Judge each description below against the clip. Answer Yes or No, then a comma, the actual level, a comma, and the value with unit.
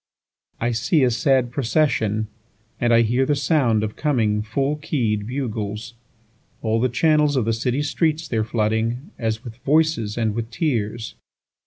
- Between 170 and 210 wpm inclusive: No, average, 140 wpm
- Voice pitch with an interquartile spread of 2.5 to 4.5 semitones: Yes, average, 4.0 semitones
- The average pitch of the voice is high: No, low, 115 Hz